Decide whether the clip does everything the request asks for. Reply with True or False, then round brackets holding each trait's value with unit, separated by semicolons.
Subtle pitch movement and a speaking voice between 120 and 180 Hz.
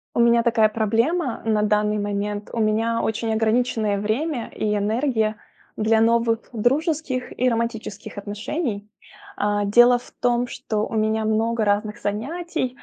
False (2.3 semitones; 225 Hz)